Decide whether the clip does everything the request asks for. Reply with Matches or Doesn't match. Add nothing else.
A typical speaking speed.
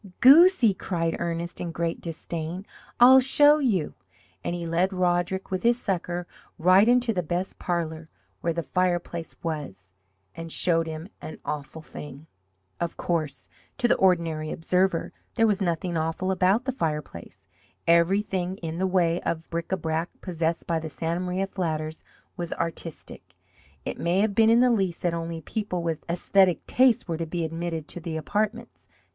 Matches